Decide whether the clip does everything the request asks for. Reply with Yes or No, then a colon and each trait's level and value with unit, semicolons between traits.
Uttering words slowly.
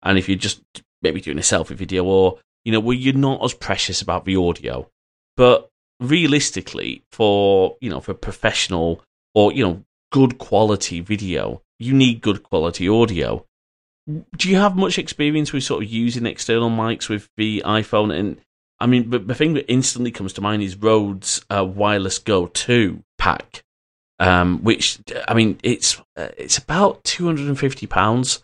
No: average, 170 wpm